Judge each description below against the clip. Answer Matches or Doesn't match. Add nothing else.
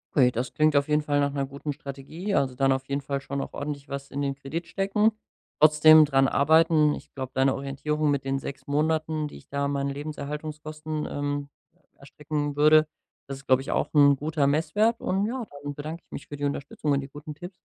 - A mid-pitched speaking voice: Matches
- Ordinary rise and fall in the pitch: Doesn't match